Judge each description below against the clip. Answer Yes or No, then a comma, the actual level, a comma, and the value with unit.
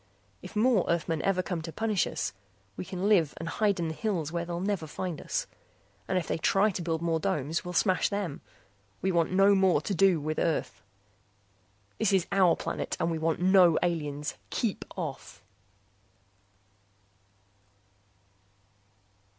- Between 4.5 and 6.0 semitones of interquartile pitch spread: No, average, 3.2 semitones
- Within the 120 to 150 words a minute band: No, average, 160 wpm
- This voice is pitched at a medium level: Yes, medium, 175 Hz